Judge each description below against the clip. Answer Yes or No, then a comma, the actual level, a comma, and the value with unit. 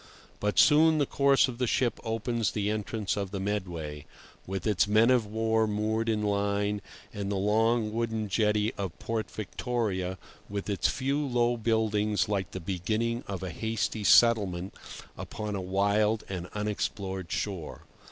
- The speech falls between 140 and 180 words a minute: Yes, average, 155 wpm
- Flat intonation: Yes, narrow, 2.3 semitones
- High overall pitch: No, low, 105 Hz